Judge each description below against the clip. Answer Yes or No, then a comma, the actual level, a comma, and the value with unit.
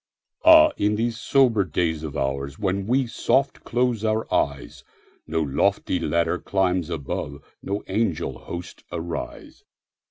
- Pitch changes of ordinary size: No, wide, 6.3 semitones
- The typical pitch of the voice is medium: No, very low, 95 Hz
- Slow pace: Yes, slow, 115 wpm